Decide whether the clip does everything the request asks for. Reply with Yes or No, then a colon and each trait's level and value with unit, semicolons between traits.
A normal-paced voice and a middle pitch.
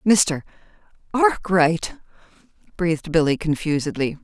No: slow, 55 wpm; medium, 170 Hz